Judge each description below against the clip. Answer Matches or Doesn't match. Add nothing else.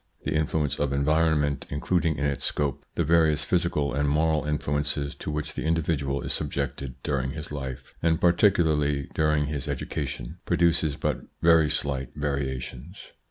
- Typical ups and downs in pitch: Doesn't match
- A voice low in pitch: Matches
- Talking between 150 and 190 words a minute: Matches